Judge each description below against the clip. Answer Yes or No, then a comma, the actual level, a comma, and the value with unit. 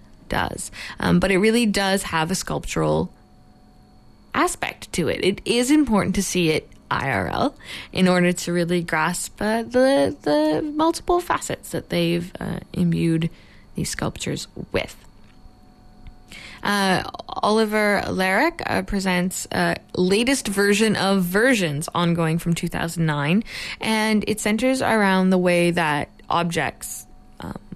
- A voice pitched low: No, medium, 185 Hz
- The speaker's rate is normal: No, slow, 130 wpm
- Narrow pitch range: No, average, 3.7 semitones